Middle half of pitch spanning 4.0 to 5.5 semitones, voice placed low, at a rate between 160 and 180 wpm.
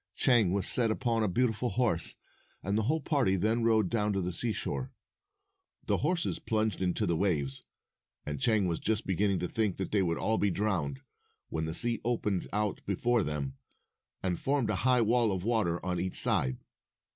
No: average, 4.5 semitones; low, 105 Hz; average, 190 wpm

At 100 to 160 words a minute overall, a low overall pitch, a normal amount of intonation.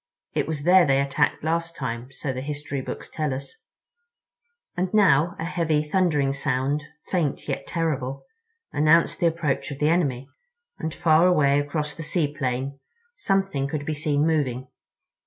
No: average, 155 wpm; medium, 150 Hz; average, 3.3 semitones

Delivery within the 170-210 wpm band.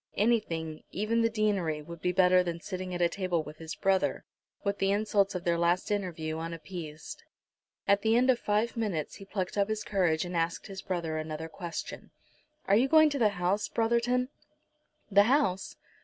Yes: average, 180 wpm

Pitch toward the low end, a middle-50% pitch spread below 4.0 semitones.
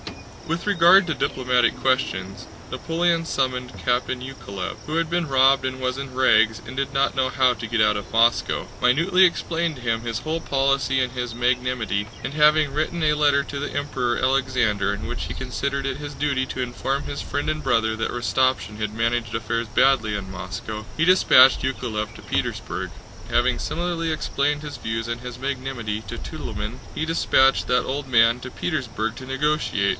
Yes: low, 130 Hz; average, 3.6 semitones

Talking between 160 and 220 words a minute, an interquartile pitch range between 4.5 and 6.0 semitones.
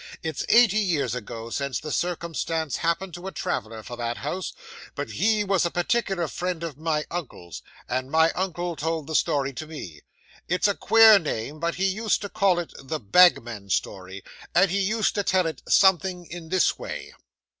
Yes: average, 185 wpm; average, 5.1 semitones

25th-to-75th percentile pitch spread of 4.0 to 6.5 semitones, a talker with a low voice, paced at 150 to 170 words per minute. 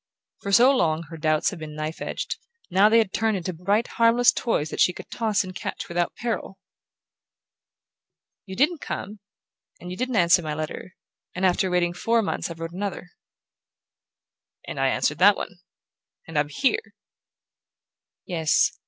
No: average, 5.2 semitones; medium, 185 Hz; average, 160 wpm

